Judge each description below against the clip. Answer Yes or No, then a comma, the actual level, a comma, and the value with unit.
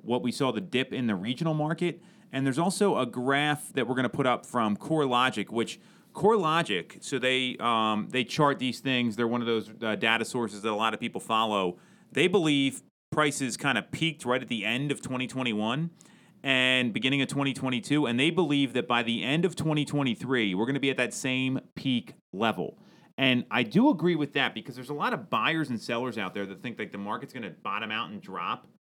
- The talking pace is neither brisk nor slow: No, fast, 220 wpm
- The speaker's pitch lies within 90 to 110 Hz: No, low, 130 Hz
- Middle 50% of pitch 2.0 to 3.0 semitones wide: No, average, 3.6 semitones